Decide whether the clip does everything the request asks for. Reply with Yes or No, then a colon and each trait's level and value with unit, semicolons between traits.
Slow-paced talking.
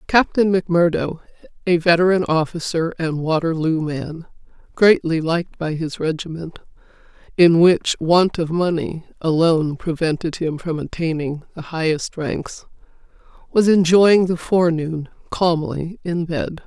Yes: slow, 120 wpm